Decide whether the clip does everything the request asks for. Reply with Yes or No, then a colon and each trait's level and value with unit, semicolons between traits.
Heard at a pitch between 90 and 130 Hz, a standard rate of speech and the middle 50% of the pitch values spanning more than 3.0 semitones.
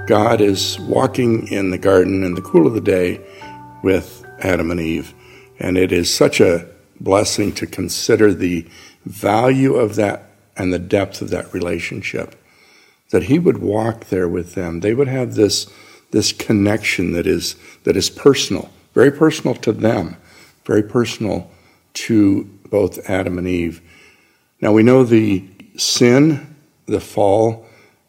Yes: low, 100 Hz; average, 150 wpm; average, 4.2 semitones